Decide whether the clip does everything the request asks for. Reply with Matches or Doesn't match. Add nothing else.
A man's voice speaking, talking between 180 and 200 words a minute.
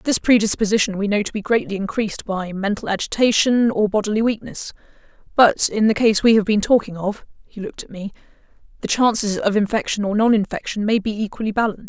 Doesn't match